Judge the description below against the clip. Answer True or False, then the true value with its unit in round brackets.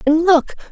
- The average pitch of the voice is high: True (325 Hz)